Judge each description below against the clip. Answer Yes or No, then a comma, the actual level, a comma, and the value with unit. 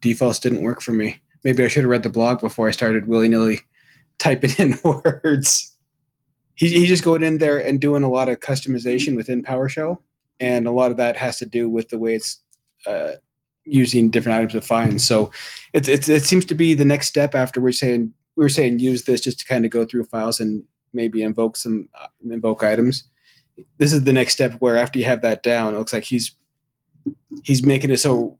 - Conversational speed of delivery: No, fast, 215 wpm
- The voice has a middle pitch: No, low, 125 Hz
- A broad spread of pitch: No, average, 3.6 semitones